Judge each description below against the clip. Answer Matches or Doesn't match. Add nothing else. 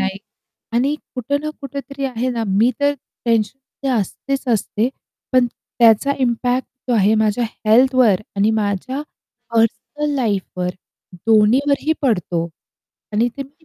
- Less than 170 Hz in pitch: Doesn't match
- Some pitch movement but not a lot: Matches